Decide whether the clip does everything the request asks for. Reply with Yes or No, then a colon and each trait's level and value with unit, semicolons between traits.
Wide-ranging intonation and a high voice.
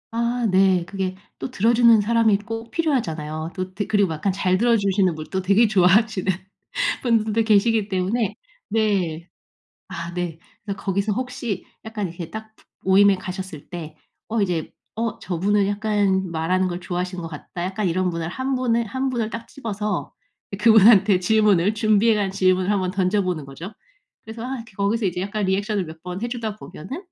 No: average, 3.3 semitones; high, 200 Hz